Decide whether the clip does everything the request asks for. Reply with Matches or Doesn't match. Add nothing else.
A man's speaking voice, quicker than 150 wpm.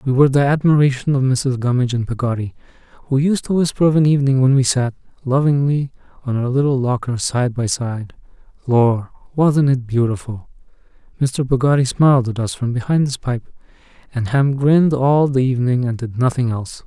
Matches